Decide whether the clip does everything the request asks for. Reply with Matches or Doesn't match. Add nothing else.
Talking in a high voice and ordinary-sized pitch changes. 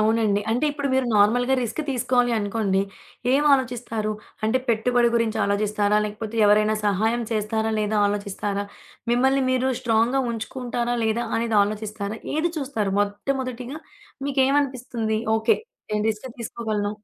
Matches